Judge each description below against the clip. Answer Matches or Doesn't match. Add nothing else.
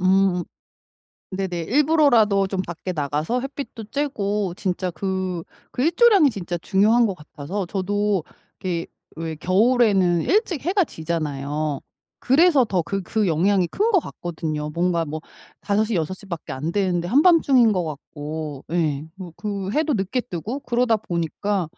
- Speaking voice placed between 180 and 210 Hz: Matches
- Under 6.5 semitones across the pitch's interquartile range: Matches